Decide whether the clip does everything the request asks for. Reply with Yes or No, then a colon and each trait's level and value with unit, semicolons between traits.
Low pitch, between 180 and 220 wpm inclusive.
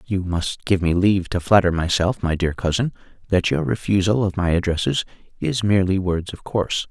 Yes: very low, 95 Hz; average, 190 wpm